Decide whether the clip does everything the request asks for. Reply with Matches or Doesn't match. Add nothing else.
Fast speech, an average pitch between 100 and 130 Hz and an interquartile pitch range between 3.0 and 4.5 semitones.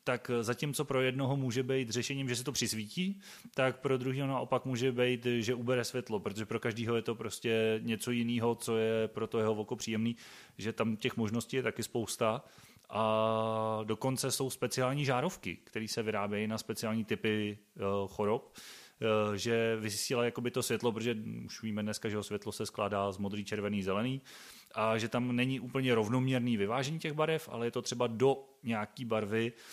Doesn't match